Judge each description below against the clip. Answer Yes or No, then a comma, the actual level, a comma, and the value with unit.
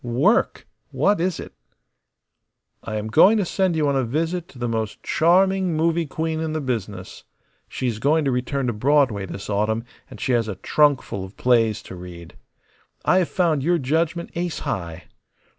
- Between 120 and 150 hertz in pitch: Yes, medium, 140 Hz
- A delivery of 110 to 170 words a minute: No, average, 180 wpm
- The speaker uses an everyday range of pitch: No, wide, 7.2 semitones